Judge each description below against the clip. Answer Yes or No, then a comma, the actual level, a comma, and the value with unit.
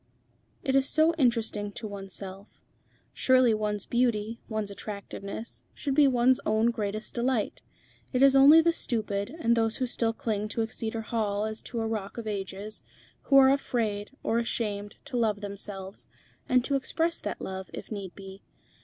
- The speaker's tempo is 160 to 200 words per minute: Yes, average, 165 wpm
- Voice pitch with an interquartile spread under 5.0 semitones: Yes, average, 3.6 semitones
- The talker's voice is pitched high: Yes, high, 225 Hz